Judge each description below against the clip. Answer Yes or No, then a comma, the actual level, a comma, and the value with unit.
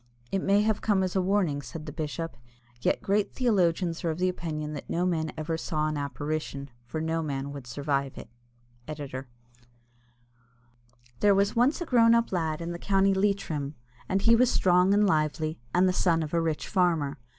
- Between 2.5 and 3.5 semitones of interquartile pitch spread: No, average, 4.3 semitones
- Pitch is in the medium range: Yes, medium, 165 Hz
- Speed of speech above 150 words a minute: Yes, average, 185 wpm